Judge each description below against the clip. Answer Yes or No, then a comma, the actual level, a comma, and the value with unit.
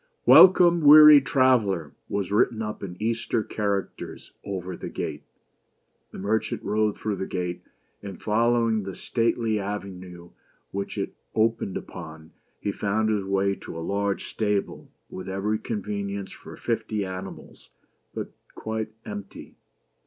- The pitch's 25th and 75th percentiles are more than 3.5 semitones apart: No, narrow, 2.4 semitones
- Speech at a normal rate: No, slow, 130 wpm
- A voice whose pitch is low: Yes, low, 100 Hz